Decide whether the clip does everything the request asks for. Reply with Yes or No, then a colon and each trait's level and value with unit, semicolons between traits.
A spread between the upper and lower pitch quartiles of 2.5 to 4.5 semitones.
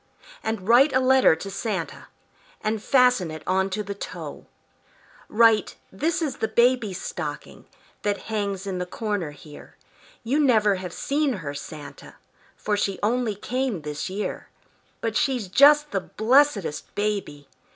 No: average, 5.0 semitones